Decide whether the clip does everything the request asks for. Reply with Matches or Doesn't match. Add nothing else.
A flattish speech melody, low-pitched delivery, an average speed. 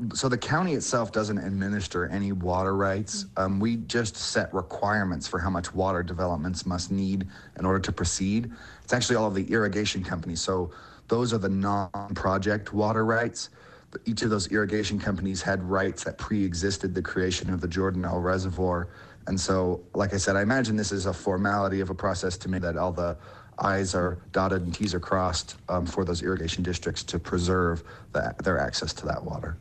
Matches